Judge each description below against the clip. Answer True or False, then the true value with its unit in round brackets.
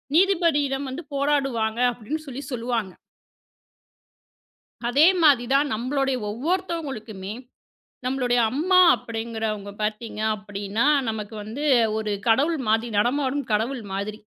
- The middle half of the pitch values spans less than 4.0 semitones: False (4.7 semitones)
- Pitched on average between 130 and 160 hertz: False (245 Hz)